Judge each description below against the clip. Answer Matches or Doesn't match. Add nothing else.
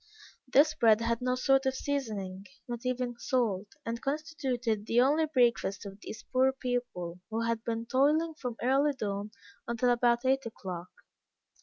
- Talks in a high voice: Matches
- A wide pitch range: Doesn't match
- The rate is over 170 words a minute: Doesn't match